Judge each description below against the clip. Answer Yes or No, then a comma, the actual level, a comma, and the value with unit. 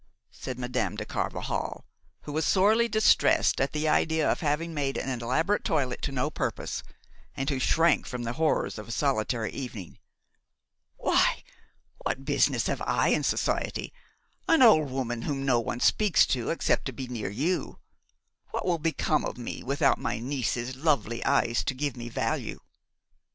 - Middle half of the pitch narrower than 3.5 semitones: No, average, 4.3 semitones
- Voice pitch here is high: No, low, 135 Hz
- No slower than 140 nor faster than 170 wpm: Yes, average, 165 wpm